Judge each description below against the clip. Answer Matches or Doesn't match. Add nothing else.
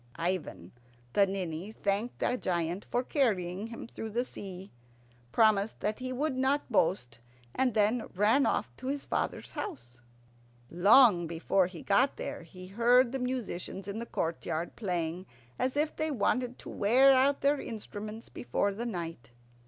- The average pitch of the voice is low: Doesn't match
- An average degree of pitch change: Doesn't match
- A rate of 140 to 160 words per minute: Matches